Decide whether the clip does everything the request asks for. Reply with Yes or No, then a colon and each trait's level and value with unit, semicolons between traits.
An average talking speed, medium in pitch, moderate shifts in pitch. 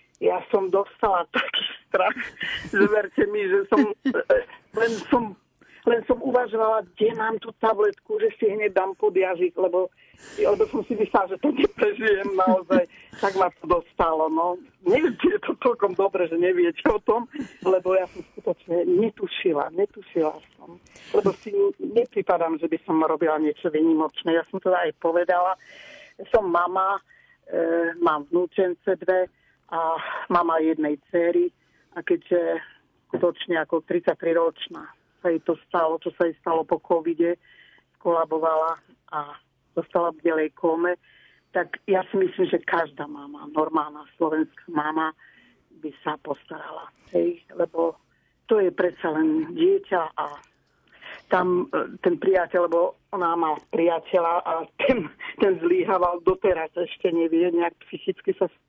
Yes: average, 140 wpm; medium, 180 Hz; average, 5.0 semitones